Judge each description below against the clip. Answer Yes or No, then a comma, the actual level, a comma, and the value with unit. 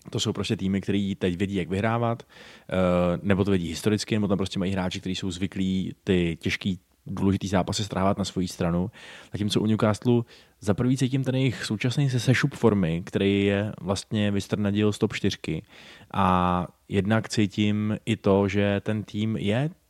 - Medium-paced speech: No, fast, 175 wpm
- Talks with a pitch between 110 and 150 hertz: No, low, 100 Hz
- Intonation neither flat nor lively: No, narrow, 2.3 semitones